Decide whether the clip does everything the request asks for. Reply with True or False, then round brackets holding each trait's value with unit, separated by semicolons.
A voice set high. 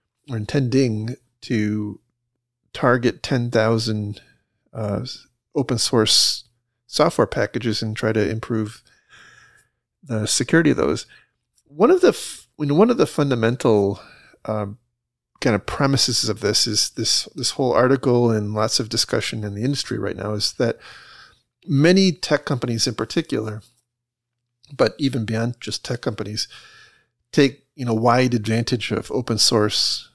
False (120 Hz)